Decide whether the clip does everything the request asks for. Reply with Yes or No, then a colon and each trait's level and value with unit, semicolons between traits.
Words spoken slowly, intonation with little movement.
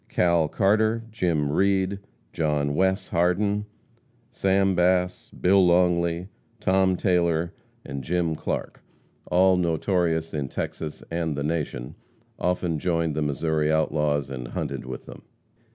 No: slow, 120 wpm; average, 3.3 semitones